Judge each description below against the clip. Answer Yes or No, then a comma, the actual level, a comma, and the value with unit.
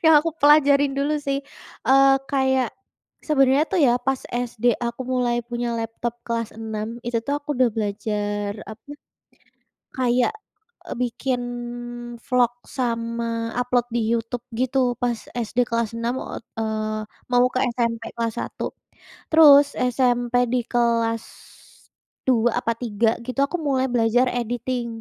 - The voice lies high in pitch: Yes, high, 240 Hz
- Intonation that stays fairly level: Yes, narrow, 2.1 semitones